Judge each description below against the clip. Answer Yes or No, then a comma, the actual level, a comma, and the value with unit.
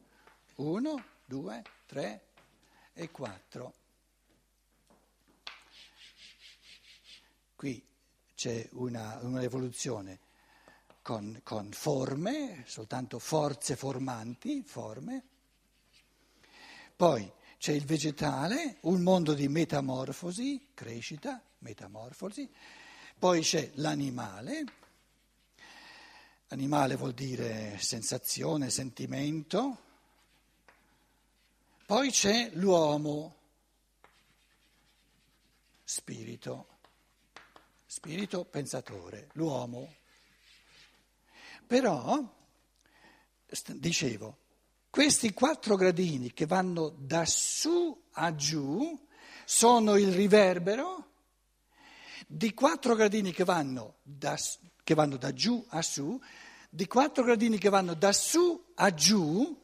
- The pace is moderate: No, slow, 80 wpm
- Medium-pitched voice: Yes, medium, 165 Hz